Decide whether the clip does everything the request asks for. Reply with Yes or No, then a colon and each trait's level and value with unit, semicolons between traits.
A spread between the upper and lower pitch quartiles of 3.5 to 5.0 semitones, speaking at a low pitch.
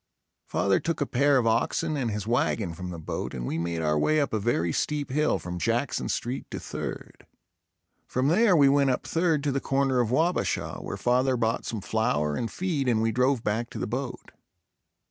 Yes: average, 4.7 semitones; low, 125 Hz